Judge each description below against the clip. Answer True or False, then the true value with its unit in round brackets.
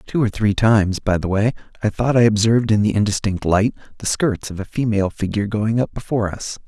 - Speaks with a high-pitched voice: False (105 Hz)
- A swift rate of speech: True (225 wpm)